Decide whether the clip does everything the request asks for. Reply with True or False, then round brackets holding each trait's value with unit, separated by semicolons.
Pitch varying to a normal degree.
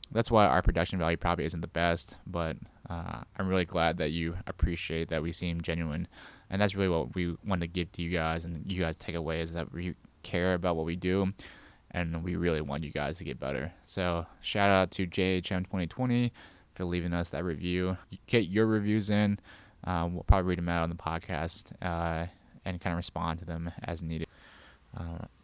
False (2.1 semitones)